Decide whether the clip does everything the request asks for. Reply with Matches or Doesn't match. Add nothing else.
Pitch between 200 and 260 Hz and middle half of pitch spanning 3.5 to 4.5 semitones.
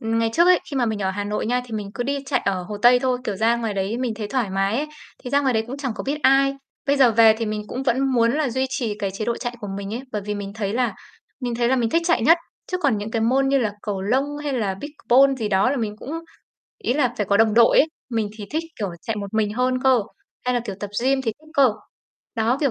Matches